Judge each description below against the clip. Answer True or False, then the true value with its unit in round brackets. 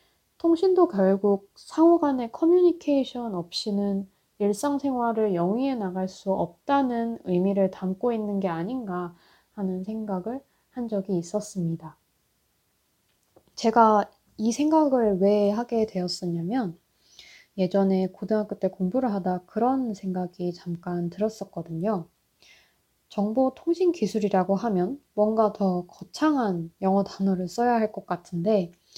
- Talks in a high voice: True (205 Hz)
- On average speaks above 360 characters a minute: False (260 characters per minute)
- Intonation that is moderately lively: True (4.3 semitones)